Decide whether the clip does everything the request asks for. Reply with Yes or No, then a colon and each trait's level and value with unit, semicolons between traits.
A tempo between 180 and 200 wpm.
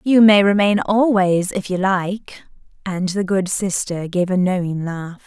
No: average, 170 wpm